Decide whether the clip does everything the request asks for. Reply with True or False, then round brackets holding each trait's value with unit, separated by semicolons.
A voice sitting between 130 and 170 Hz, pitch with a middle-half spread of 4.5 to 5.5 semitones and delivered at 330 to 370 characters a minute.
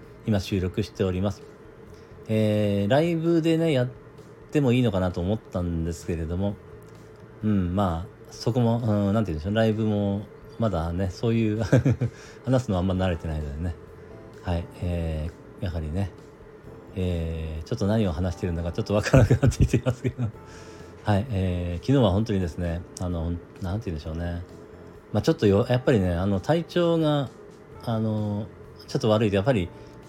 False (105 Hz; 5.1 semitones; 350 characters per minute)